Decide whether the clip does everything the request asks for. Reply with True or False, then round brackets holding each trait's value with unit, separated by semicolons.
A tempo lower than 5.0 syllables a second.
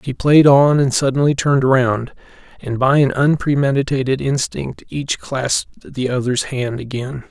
True (4.5 syllables/s)